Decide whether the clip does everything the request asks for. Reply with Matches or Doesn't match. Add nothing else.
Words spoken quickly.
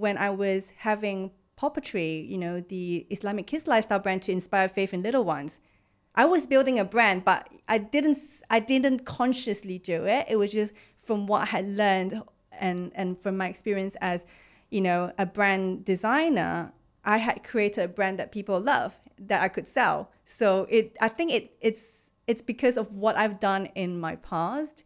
Doesn't match